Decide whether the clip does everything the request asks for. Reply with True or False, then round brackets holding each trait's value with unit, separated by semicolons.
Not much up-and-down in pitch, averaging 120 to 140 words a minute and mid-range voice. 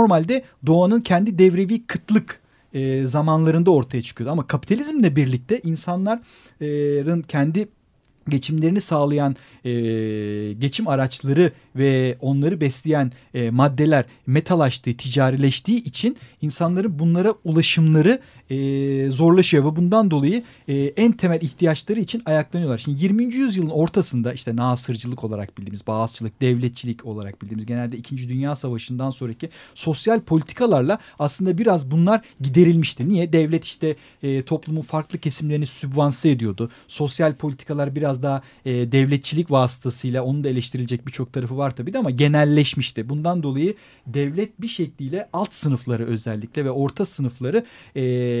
False (4.7 semitones; 130 wpm; 145 Hz)